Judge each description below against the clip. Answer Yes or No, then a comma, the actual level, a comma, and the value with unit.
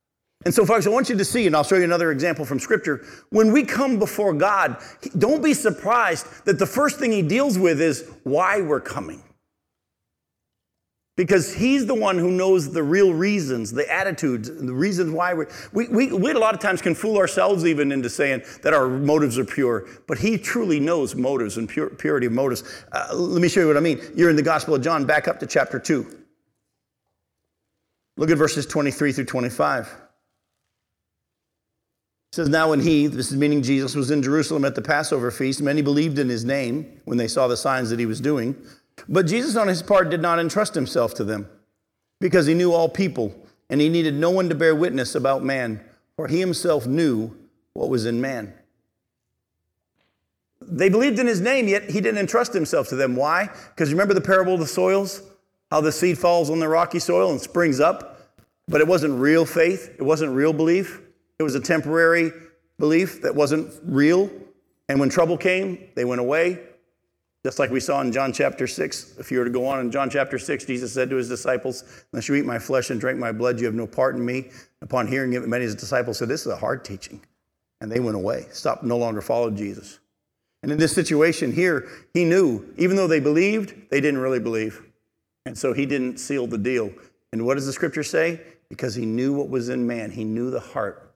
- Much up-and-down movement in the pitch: Yes, wide, 6.2 semitones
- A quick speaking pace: Yes, fast, 215 wpm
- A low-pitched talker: No, medium, 155 Hz